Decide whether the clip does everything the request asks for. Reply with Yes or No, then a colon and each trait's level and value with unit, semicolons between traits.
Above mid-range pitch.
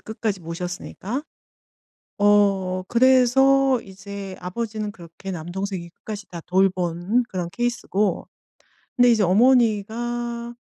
Yes: high, 205 Hz